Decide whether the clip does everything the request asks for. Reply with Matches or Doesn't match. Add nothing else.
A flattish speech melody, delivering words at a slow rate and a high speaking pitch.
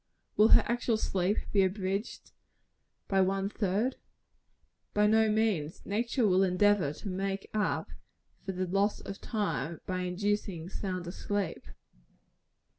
Matches